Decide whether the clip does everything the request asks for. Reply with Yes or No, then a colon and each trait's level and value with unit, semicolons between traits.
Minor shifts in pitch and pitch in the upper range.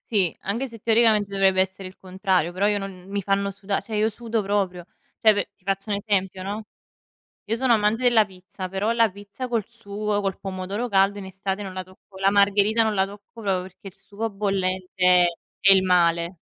Yes: narrow, 2.0 semitones; high, 200 Hz